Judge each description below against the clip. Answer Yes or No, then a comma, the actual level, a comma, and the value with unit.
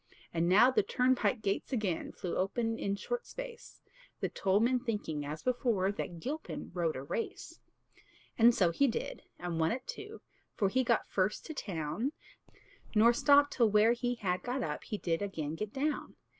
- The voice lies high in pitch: Yes, high, 215 Hz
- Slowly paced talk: No, average, 180 wpm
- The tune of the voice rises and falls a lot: Yes, wide, 5.7 semitones